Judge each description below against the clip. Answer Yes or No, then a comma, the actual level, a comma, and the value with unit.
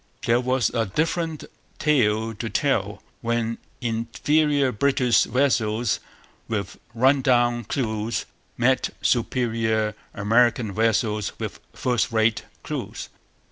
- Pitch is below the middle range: Yes, low, 115 Hz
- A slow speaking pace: Yes, slow, 100 wpm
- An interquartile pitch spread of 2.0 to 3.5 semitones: Yes, average, 2.7 semitones